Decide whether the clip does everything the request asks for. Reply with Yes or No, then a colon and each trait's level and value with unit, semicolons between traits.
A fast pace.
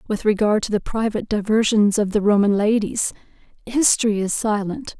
No: average, 155 wpm